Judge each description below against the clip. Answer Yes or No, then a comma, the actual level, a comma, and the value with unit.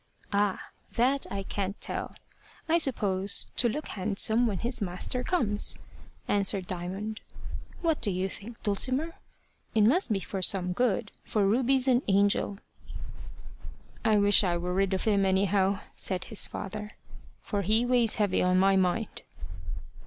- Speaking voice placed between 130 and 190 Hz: No, high, 205 Hz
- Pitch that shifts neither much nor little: Yes, average, 3.5 semitones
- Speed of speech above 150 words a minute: No, average, 145 wpm